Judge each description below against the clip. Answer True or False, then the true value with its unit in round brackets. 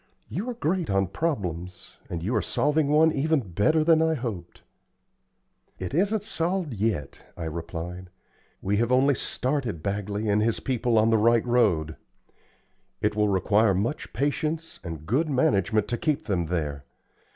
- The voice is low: True (110 Hz)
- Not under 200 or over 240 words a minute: False (155 wpm)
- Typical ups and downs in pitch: False (8.1 semitones)